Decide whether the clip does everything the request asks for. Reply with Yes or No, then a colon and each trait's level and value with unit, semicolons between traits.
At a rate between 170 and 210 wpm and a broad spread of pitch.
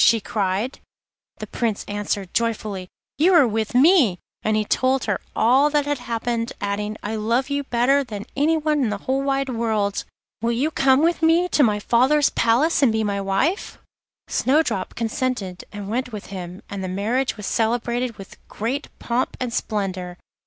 No: average, 175 wpm; average, 4.7 semitones